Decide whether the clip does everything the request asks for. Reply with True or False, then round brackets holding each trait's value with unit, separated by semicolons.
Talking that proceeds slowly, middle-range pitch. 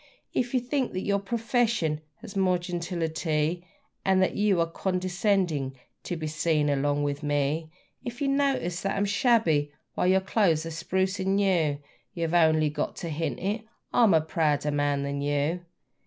False (175 wpm; 175 Hz)